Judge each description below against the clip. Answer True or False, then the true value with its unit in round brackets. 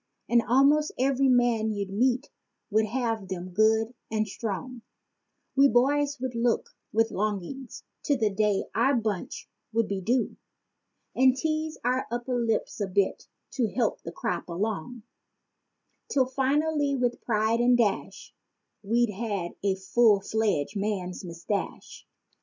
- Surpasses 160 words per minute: False (140 wpm)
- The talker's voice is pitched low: False (230 Hz)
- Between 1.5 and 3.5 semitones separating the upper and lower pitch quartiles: False (3.9 semitones)